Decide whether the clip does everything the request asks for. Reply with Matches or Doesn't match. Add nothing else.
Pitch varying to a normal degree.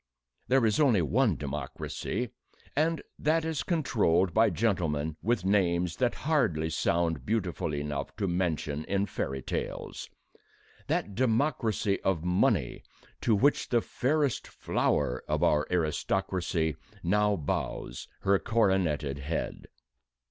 Doesn't match